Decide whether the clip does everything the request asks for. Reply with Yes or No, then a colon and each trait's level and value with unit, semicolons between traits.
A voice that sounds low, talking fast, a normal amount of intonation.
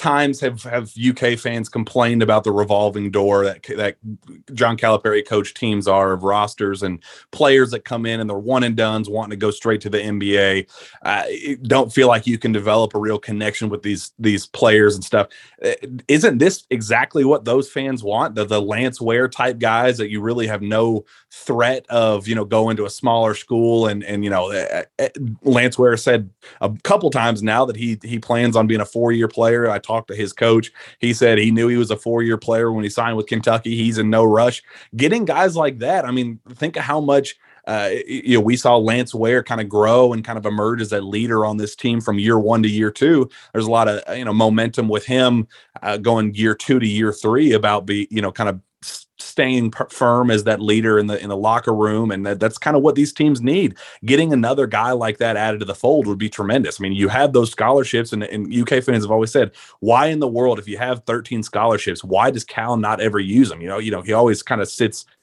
No: low, 115 Hz; fast, 230 wpm; narrow, 2.3 semitones